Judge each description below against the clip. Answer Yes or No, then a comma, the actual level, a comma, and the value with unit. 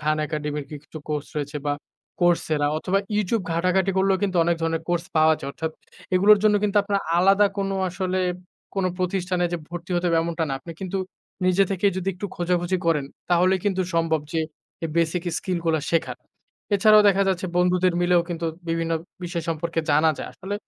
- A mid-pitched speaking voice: Yes, medium, 175 Hz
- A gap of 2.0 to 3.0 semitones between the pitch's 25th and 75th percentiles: Yes, narrow, 2.5 semitones